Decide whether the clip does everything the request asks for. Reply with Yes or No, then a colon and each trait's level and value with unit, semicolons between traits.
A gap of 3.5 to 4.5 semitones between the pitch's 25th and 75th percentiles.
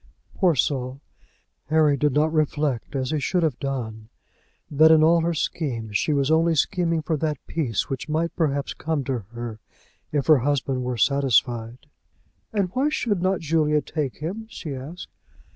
Yes: average, 3.8 semitones